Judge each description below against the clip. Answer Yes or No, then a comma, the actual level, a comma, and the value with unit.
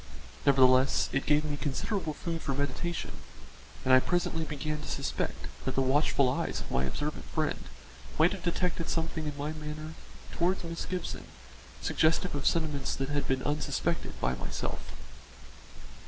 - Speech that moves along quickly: No, average, 155 wpm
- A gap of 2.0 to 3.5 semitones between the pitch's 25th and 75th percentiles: Yes, average, 3.0 semitones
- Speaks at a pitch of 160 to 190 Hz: No, medium, 150 Hz